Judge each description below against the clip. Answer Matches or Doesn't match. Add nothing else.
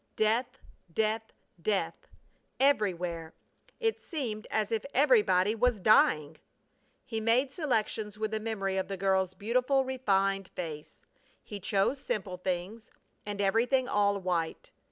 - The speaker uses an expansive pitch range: Doesn't match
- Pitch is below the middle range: Doesn't match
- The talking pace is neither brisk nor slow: Doesn't match